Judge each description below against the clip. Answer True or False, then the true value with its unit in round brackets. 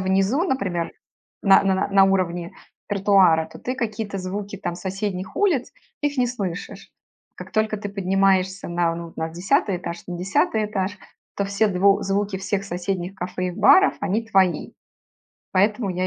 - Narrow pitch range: True (2.1 semitones)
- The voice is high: True (195 Hz)